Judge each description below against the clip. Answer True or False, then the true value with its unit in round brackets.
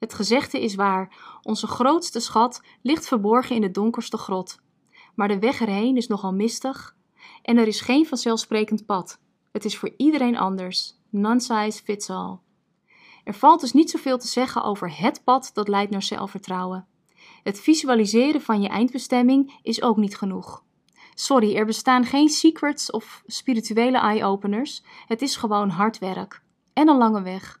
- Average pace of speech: True (165 wpm)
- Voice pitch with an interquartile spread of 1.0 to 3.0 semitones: False (3.9 semitones)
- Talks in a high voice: True (225 Hz)